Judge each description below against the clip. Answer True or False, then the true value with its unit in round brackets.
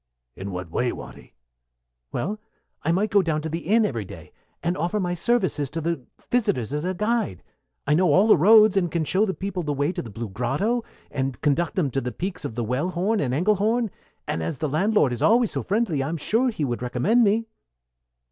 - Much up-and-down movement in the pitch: True (7.5 semitones)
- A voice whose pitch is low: False (170 Hz)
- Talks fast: True (215 wpm)